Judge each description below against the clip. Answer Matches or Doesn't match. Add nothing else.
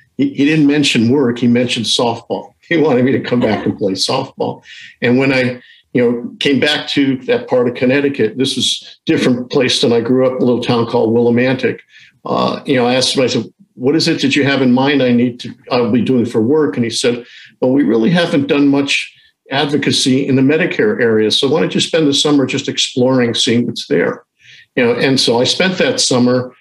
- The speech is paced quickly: Matches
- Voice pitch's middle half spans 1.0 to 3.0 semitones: Matches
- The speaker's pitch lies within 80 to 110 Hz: Doesn't match